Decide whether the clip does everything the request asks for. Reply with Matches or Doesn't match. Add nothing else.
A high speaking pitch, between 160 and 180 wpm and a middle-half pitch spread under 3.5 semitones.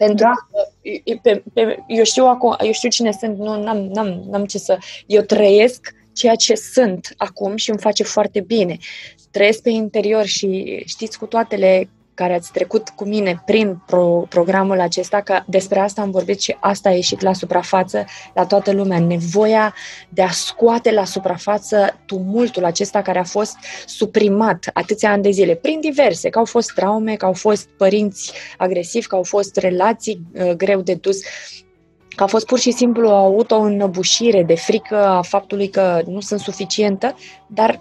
Matches